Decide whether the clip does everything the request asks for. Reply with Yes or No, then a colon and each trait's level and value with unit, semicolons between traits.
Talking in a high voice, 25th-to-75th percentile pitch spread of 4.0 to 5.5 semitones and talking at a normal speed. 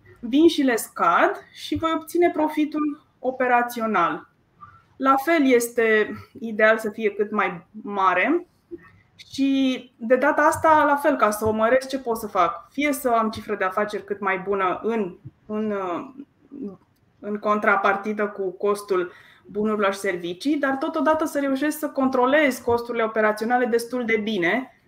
Yes: high, 235 Hz; average, 5.1 semitones; average, 145 wpm